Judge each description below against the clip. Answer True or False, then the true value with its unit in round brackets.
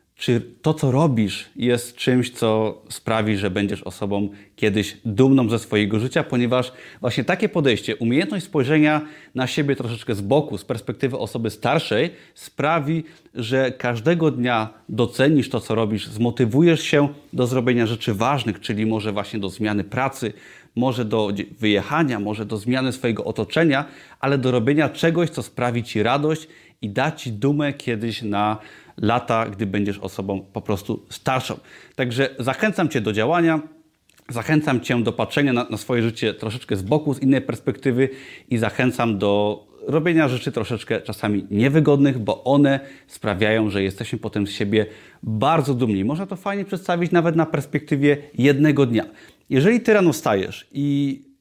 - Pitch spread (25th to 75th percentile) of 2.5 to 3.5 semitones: False (4.8 semitones)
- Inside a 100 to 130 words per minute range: False (150 wpm)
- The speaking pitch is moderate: False (125 Hz)